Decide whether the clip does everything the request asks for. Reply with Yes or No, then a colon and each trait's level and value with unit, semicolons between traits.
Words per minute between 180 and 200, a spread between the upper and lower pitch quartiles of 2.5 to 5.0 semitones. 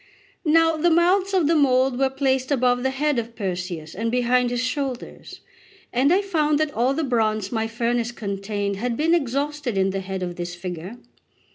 No: average, 185 wpm; wide, 5.5 semitones